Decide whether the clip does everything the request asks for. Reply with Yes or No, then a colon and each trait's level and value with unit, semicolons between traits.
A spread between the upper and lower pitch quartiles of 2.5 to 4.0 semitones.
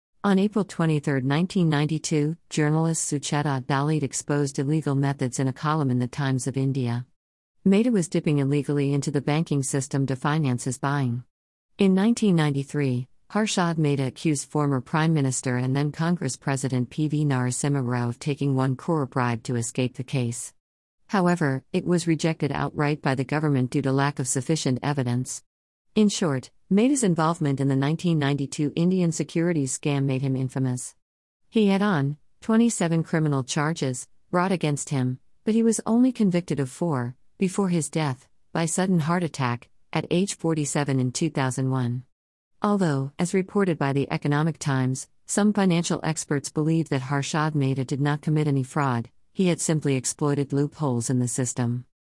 Yes: average, 3.7 semitones